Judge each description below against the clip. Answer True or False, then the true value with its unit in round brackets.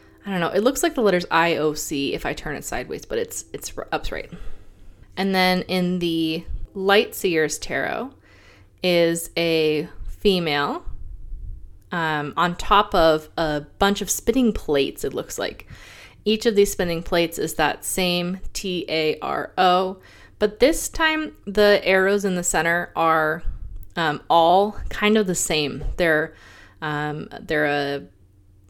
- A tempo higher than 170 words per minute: False (145 wpm)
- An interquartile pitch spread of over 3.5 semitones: True (4.6 semitones)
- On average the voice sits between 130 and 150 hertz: False (170 Hz)